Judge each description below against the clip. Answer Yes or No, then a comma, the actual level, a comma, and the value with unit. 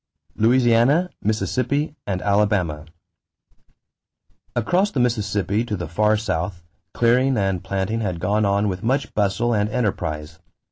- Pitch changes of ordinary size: Yes, average, 3.9 semitones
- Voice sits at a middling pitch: No, low, 105 Hz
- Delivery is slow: Yes, slow, 125 wpm